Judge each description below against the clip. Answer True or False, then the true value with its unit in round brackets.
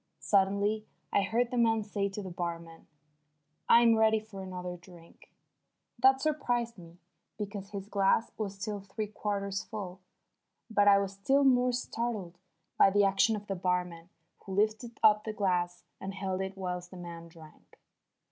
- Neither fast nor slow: True (160 wpm)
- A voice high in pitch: True (200 Hz)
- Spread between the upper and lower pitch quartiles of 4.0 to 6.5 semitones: False (3.1 semitones)